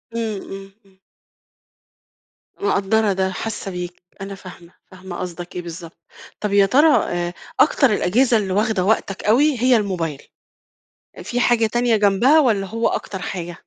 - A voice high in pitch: Yes, high, 195 Hz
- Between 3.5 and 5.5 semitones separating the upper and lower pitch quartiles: Yes, average, 3.8 semitones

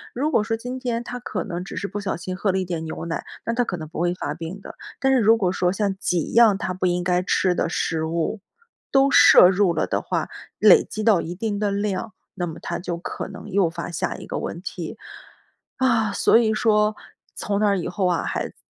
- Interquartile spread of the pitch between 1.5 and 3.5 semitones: No, average, 3.9 semitones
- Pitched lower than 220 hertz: Yes, high, 195 Hz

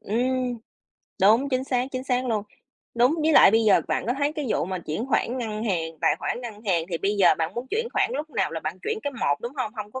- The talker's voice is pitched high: Yes, high, 235 Hz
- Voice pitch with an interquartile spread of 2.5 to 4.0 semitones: No, average, 4.8 semitones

